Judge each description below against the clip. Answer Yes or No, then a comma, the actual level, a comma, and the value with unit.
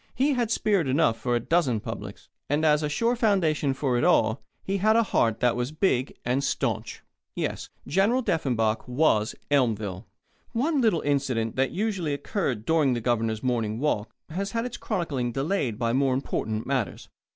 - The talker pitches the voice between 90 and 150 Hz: Yes, medium, 140 Hz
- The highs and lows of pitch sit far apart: Yes, wide, 7.9 semitones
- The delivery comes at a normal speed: Yes, average, 175 wpm